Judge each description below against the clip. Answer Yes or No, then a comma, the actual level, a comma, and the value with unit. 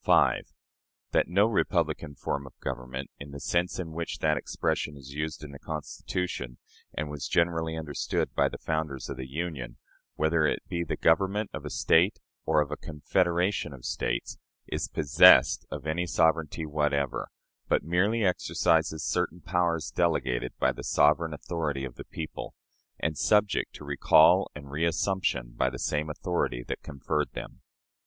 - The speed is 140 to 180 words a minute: Yes, average, 160 wpm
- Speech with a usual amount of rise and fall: Yes, average, 3.2 semitones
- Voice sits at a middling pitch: No, very low, 80 Hz